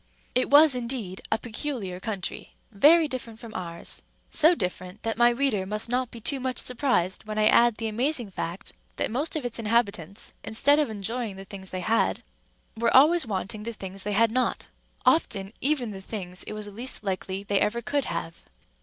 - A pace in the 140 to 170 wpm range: No, average, 185 wpm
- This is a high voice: Yes, high, 225 Hz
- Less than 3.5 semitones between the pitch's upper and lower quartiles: No, average, 4.3 semitones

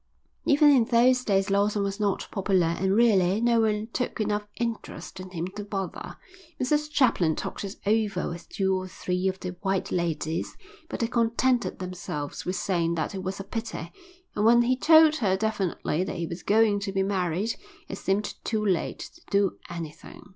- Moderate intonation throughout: Yes, average, 3.5 semitones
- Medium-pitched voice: No, high, 200 Hz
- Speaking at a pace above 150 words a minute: Yes, average, 185 wpm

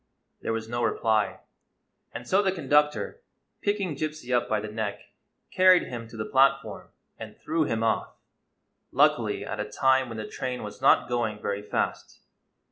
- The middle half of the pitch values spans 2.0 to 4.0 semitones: No, average, 5.1 semitones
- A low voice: Yes, low, 120 Hz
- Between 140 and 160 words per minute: No, average, 170 wpm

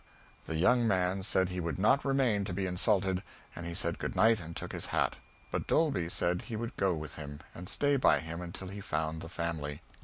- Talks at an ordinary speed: No, fast, 220 wpm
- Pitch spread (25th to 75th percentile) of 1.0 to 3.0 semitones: No, average, 4.1 semitones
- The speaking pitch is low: Yes, very low, 90 Hz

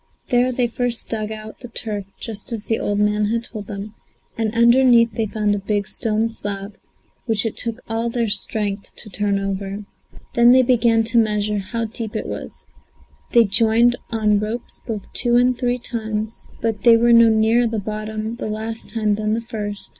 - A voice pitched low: No, high, 220 Hz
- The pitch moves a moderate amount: No, narrow, 1.8 semitones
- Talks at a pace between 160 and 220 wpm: Yes, average, 190 wpm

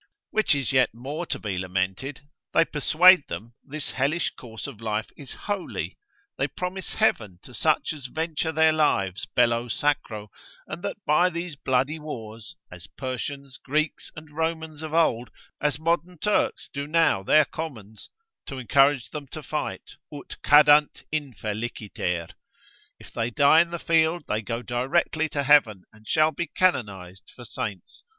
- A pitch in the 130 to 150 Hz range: Yes, medium, 140 Hz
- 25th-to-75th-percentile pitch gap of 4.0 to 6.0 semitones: Yes, wide, 5.5 semitones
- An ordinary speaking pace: Yes, average, 155 wpm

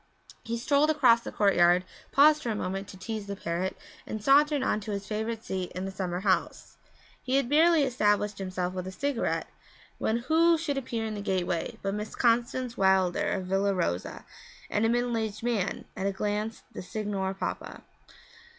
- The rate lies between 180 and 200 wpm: Yes, average, 185 wpm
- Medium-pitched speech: No, high, 210 Hz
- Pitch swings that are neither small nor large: Yes, average, 4.2 semitones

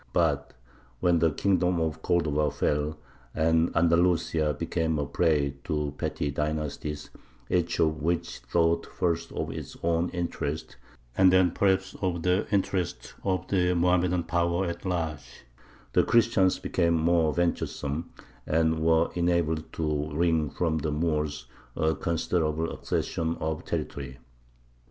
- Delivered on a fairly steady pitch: Yes, narrow, 2.2 semitones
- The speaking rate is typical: No, slow, 130 wpm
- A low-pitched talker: Yes, very low, 80 Hz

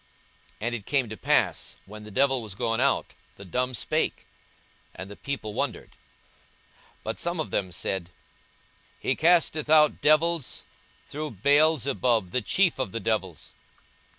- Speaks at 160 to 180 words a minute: No, average, 150 wpm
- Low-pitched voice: Yes, low, 125 Hz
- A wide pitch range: Yes, wide, 6.2 semitones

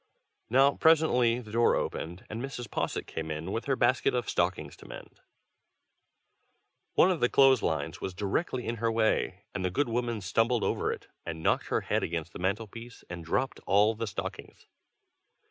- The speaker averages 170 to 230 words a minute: Yes, average, 180 wpm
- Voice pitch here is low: Yes, low, 115 Hz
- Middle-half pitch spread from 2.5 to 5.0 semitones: No, wide, 5.4 semitones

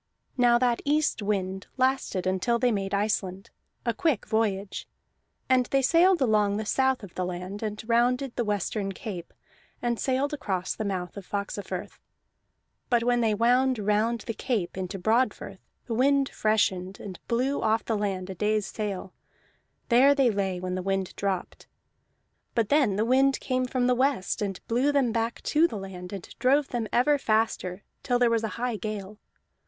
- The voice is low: No, high, 220 Hz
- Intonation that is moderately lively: Yes, average, 4.3 semitones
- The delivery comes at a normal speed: Yes, average, 175 wpm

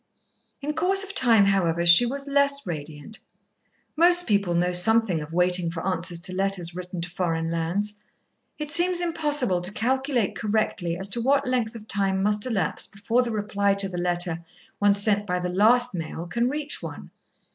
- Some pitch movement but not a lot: No, wide, 5.8 semitones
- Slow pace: No, average, 180 wpm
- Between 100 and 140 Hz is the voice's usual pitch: No, high, 200 Hz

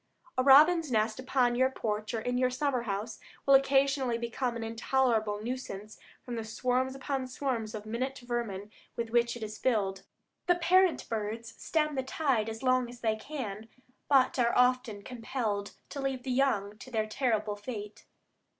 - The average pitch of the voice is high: Yes, high, 240 Hz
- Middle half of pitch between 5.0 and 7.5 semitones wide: No, average, 3.3 semitones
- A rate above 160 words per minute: Yes, average, 170 wpm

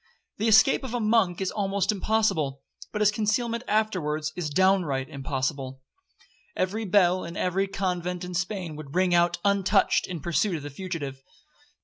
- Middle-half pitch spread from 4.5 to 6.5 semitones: Yes, average, 5.0 semitones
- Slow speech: No, average, 150 wpm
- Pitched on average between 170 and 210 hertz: Yes, medium, 185 Hz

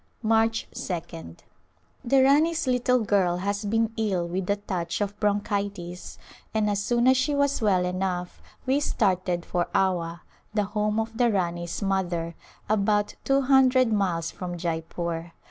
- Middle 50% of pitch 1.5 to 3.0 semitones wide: No, average, 4.3 semitones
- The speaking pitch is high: Yes, high, 200 Hz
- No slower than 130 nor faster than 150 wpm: Yes, average, 145 wpm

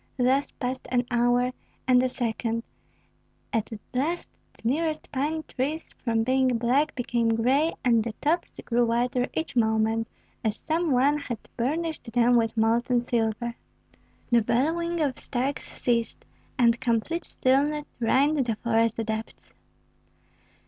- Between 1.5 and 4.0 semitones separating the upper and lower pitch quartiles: Yes, average, 3.6 semitones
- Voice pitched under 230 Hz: No, high, 245 Hz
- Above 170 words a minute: No, average, 140 wpm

